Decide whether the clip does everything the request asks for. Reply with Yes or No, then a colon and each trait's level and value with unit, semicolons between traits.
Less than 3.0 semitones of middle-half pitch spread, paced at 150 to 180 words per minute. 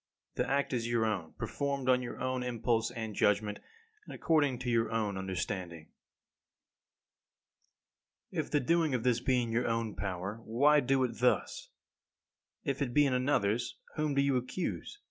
No: average, 3.7 semitones; average, 165 wpm